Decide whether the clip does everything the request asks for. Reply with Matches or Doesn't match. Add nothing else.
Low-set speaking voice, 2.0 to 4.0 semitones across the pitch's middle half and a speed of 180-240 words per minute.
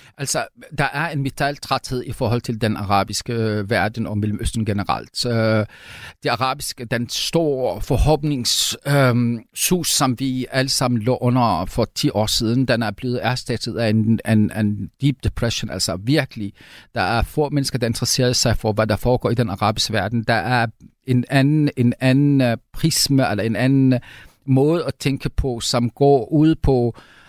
Doesn't match